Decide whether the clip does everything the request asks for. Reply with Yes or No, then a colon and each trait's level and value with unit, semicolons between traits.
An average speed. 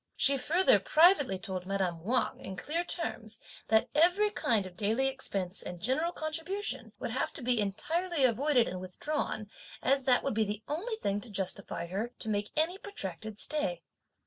Yes: average, 170 wpm